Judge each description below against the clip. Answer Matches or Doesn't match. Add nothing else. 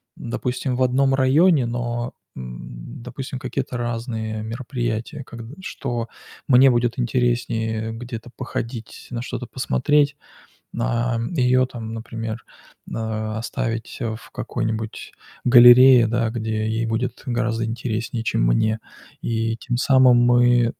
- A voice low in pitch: Matches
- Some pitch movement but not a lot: Doesn't match